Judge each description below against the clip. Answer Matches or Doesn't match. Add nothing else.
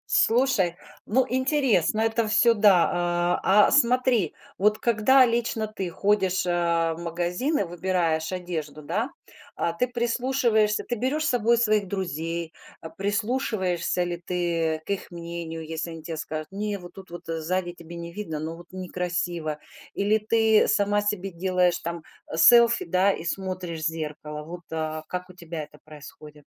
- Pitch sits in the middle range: Matches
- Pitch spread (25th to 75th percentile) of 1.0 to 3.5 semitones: Doesn't match